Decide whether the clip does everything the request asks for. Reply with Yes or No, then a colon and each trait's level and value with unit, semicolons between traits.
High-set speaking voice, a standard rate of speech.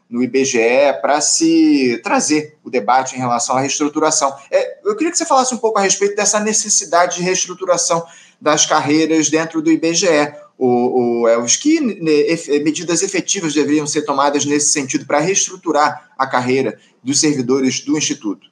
No: medium, 155 Hz; average, 155 wpm